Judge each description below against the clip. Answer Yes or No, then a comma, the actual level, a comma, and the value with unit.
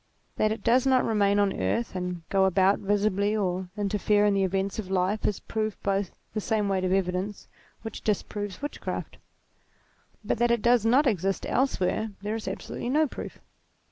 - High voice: Yes, high, 205 Hz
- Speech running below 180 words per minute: No, average, 185 wpm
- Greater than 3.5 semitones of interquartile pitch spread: No, narrow, 2.5 semitones